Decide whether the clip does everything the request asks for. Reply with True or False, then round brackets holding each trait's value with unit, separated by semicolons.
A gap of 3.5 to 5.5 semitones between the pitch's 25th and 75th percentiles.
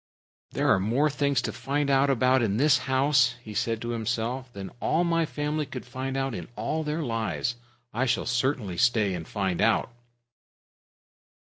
True (3.8 semitones)